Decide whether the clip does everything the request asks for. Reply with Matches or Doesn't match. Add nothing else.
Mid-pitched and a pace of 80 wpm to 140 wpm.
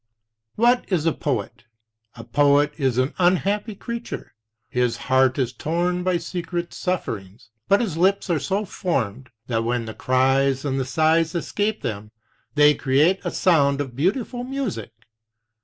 Doesn't match